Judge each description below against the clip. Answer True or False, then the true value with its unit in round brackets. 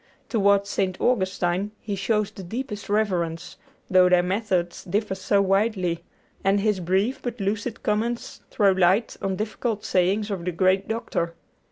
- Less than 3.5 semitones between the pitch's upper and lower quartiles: True (2.5 semitones)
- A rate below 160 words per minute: True (150 wpm)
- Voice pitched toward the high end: True (195 Hz)